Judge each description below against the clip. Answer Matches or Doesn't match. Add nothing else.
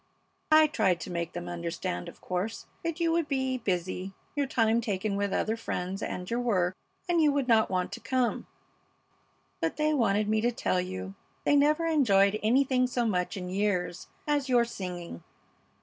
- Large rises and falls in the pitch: Matches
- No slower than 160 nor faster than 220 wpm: Matches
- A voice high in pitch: Matches